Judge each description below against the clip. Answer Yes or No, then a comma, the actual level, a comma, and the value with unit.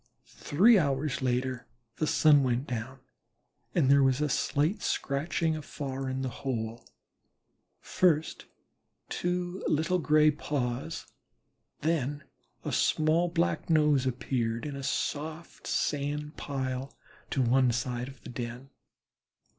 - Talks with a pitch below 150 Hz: Yes, medium, 140 Hz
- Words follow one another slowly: Yes, slow, 120 wpm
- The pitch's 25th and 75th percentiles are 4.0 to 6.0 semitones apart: No, average, 3.4 semitones